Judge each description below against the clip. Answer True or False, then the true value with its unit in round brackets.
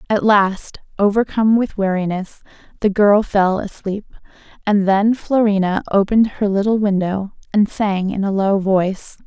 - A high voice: True (200 Hz)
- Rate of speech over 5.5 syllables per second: False (4.6 syllables/s)